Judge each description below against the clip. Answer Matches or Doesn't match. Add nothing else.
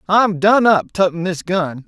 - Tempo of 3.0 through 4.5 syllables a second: Matches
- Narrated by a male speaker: Matches